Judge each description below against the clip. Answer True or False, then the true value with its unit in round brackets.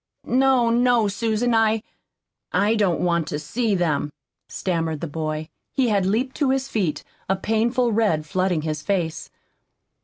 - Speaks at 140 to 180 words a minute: True (150 wpm)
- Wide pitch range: True (6.2 semitones)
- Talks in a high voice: True (205 Hz)